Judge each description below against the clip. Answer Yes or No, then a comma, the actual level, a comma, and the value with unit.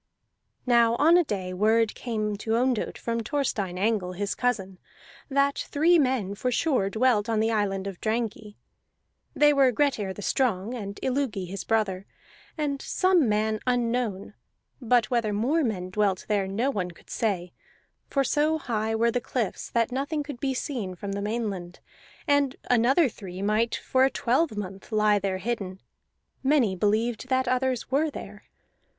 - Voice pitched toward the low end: No, high, 225 Hz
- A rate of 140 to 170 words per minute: Yes, average, 160 wpm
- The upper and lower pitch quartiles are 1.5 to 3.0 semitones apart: No, average, 4.4 semitones